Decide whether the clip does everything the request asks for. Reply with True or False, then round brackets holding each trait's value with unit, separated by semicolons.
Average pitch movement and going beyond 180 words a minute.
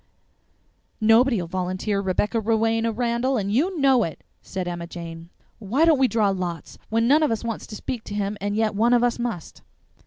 True (3.9 semitones; 190 wpm)